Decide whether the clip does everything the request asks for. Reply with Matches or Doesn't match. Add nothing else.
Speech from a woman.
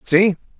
Doesn't match